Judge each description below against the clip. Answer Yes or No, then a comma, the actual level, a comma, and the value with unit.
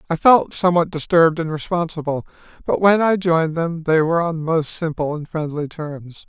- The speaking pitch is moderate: Yes, medium, 160 Hz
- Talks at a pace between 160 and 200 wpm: Yes, average, 180 wpm